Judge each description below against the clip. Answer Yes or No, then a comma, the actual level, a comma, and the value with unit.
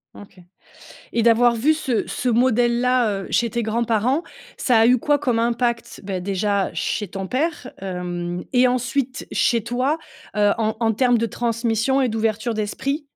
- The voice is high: Yes, high, 235 Hz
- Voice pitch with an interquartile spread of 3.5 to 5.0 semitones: No, average, 2.9 semitones